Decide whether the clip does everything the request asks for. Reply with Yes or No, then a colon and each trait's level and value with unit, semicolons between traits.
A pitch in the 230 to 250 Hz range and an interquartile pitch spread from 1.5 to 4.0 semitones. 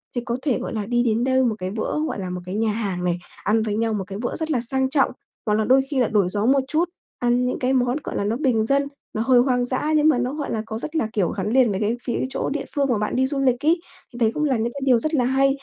Yes: high, 245 Hz; average, 3.7 semitones